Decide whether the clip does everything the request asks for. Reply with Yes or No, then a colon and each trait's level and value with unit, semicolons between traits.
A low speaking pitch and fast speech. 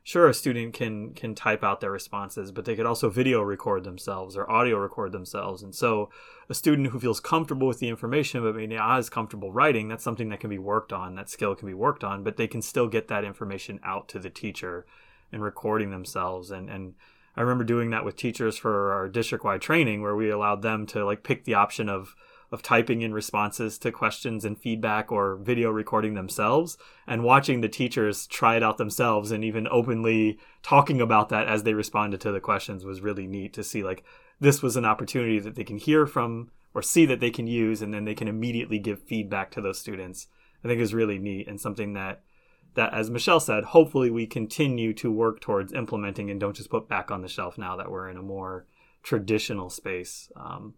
Yes: low, 110 Hz; fast, 220 wpm